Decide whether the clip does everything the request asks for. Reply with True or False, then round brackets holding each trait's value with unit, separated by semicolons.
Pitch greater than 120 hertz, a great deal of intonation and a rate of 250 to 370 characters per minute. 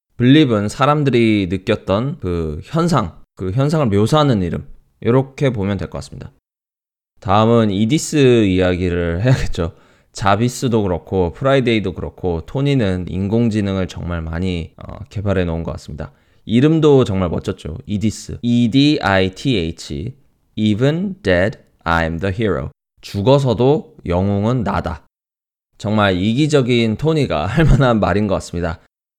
False (100 Hz; 6.1 semitones; 305 characters per minute)